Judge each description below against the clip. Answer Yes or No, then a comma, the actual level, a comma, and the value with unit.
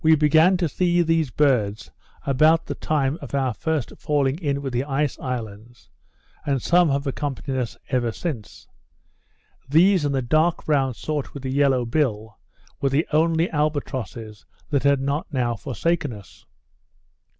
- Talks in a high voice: No, medium, 140 Hz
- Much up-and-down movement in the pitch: No, average, 3.6 semitones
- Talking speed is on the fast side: No, average, 155 wpm